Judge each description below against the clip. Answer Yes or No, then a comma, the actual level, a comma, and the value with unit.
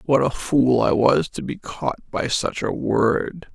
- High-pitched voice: No, medium, 155 Hz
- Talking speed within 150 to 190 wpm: No, fast, 205 wpm